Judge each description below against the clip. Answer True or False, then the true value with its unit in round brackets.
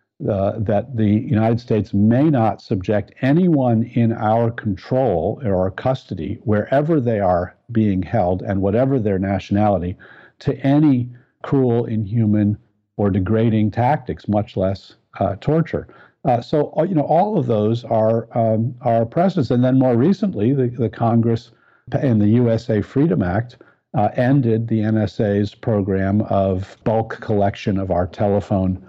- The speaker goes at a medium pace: True (145 wpm)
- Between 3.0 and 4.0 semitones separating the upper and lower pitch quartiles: True (3.4 semitones)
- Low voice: True (110 Hz)